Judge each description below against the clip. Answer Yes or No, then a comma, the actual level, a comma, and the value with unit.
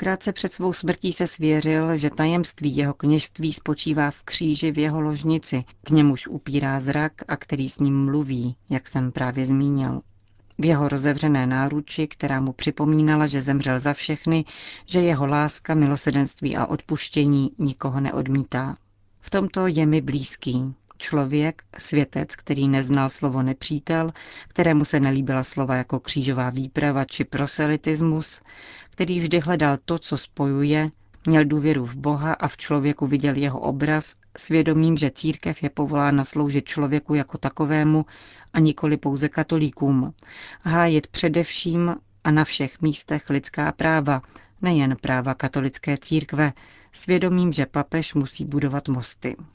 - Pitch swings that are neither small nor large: No, narrow, 2.3 semitones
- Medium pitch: Yes, medium, 145 Hz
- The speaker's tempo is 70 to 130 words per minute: No, average, 140 wpm